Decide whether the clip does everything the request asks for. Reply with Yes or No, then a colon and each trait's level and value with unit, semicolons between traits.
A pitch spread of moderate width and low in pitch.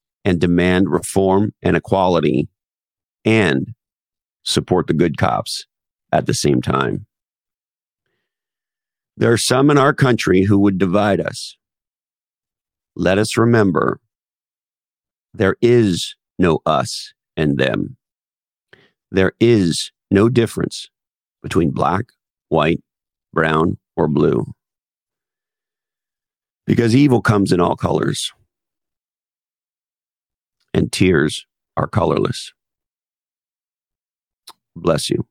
Yes: average, 4.6 semitones; low, 105 Hz